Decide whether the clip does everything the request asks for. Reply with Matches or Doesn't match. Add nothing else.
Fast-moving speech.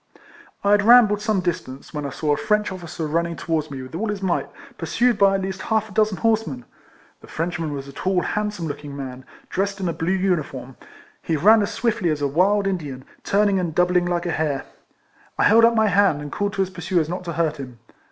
Matches